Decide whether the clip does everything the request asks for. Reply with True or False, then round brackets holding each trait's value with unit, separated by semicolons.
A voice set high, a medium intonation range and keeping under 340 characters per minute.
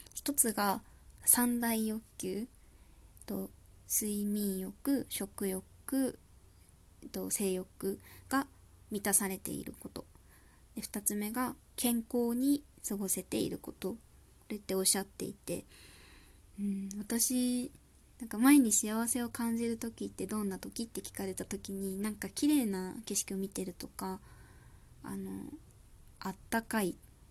True (205 Hz; 3.8 semitones; 220 characters per minute)